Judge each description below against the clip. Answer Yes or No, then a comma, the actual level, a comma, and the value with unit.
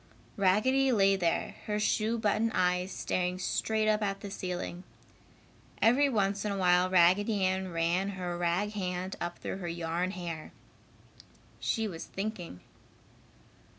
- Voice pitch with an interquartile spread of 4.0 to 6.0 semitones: No, average, 2.9 semitones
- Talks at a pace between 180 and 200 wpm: No, average, 140 wpm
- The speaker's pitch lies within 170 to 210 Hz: Yes, high, 190 Hz